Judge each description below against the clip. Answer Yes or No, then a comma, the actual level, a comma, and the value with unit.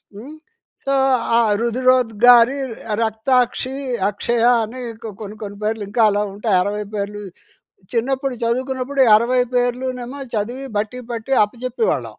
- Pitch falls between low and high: No, high, 240 Hz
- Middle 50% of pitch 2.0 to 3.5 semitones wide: Yes, average, 3.0 semitones